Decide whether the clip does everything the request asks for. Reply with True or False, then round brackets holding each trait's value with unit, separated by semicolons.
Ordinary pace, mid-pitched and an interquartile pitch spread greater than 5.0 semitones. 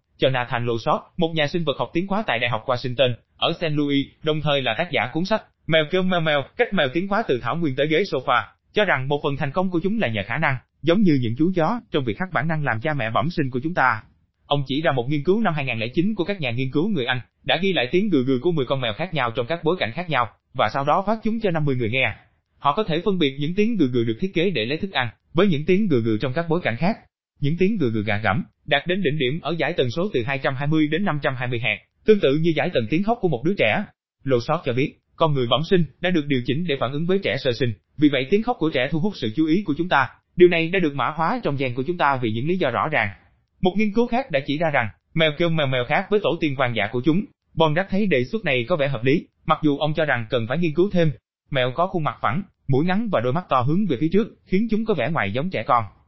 False (295 wpm; 150 Hz; 5.5 semitones)